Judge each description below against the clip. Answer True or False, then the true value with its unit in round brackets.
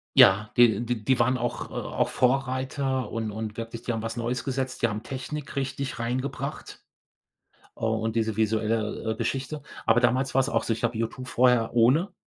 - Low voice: True (120 Hz)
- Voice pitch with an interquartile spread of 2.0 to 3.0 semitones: True (2.6 semitones)